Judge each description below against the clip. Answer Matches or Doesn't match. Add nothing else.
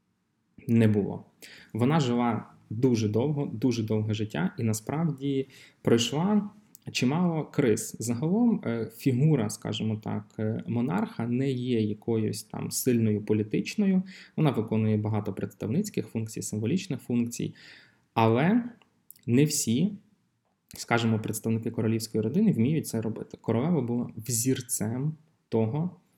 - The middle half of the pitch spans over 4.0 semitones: Matches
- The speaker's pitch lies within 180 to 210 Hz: Doesn't match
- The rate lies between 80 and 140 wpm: Matches